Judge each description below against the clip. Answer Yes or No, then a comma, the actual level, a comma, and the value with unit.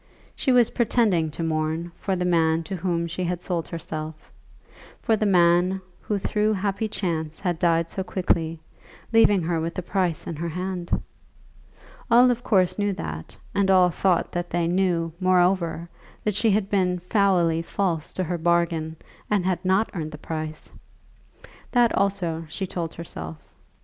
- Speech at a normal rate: Yes, average, 165 wpm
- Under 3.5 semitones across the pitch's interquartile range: Yes, average, 2.8 semitones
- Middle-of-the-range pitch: Yes, medium, 175 Hz